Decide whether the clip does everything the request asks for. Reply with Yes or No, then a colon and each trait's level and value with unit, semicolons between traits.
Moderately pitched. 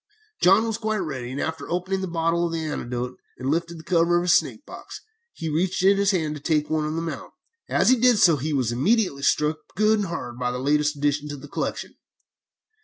Yes: medium, 165 Hz